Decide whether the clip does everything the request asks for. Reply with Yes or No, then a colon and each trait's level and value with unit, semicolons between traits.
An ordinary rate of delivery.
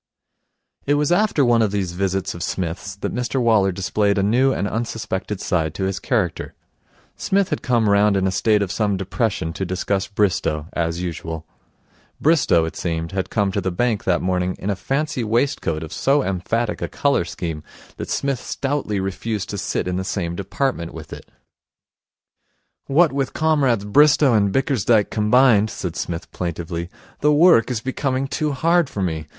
Yes: average, 175 wpm